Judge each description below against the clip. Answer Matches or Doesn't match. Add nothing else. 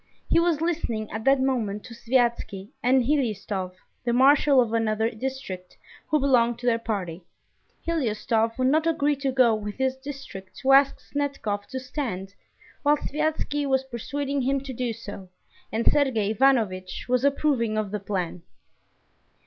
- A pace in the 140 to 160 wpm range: Matches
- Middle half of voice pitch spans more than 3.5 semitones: Matches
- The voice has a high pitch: Matches